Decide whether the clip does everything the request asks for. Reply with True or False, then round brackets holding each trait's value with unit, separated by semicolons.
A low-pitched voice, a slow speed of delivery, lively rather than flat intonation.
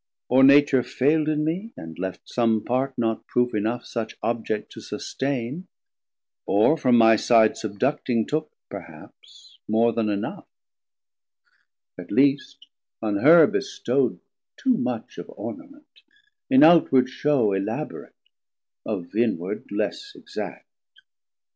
True (125 Hz; 120 wpm; 5.7 semitones)